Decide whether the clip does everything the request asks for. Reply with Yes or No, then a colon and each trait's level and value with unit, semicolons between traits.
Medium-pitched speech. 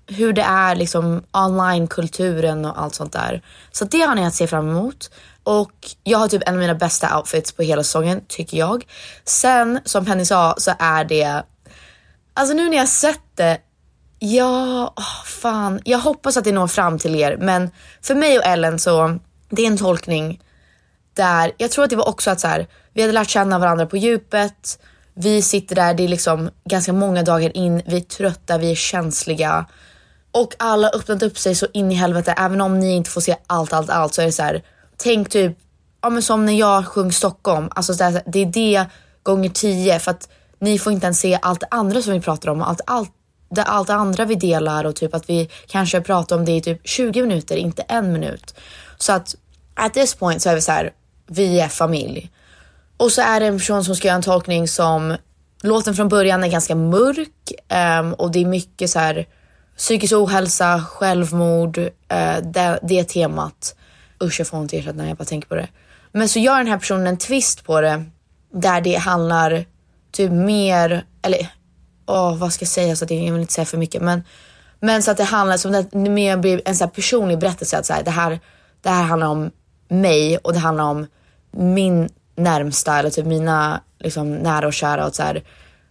Yes: medium, 180 Hz